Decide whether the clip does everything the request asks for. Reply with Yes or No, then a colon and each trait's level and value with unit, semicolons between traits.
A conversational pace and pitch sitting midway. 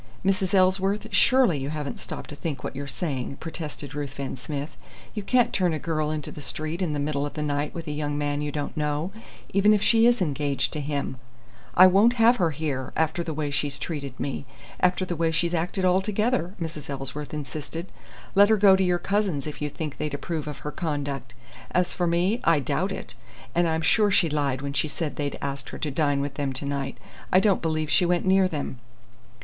No: fast, 215 wpm; medium, 155 Hz